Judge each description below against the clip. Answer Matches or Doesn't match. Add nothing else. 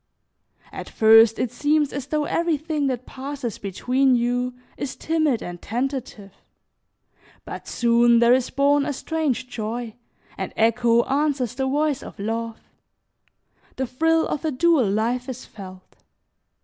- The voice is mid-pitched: Doesn't match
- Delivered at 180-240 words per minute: Doesn't match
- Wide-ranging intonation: Doesn't match